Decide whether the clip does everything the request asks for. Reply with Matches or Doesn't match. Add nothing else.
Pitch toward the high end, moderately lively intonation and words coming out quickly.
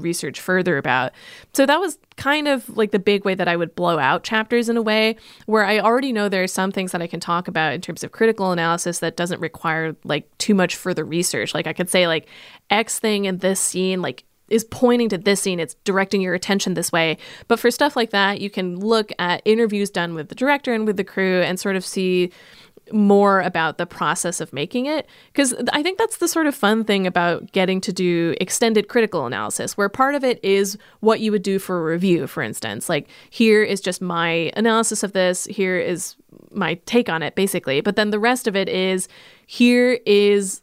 Matches